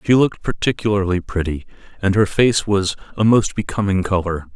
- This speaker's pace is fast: No, average, 160 wpm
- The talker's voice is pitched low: Yes, low, 100 Hz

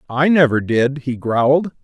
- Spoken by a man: Yes, male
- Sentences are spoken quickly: No, average, 165 wpm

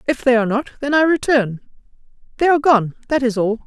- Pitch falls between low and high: No, very high, 255 Hz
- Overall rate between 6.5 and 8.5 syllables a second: Yes, 6.7 syllables/s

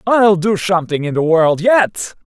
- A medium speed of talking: Yes, average, 180 wpm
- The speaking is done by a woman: No, male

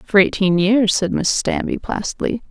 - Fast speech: No, average, 170 wpm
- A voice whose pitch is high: Yes, high, 205 Hz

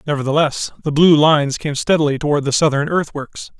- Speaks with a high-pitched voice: No, medium, 150 Hz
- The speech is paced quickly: No, average, 165 wpm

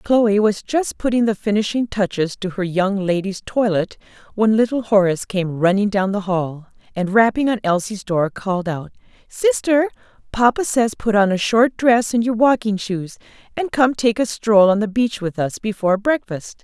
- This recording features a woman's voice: Yes, female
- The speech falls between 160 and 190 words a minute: Yes, average, 185 wpm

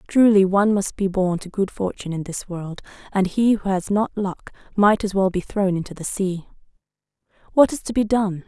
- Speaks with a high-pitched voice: Yes, high, 195 Hz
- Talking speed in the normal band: No, fast, 210 wpm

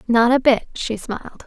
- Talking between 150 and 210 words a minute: Yes, fast, 205 wpm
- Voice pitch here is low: No, high, 235 Hz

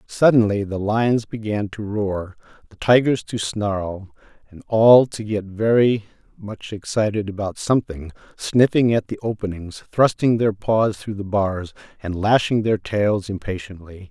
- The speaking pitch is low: Yes, low, 105 Hz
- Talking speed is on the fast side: No, average, 145 wpm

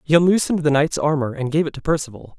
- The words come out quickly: Yes, fast, 250 wpm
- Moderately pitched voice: Yes, medium, 155 Hz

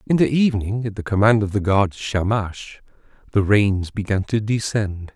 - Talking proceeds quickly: No, average, 175 wpm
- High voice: No, low, 105 Hz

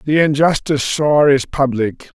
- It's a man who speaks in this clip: Yes, male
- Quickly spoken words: No, slow, 135 wpm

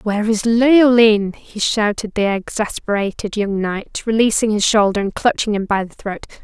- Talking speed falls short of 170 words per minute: Yes, average, 160 wpm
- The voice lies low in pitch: No, high, 210 Hz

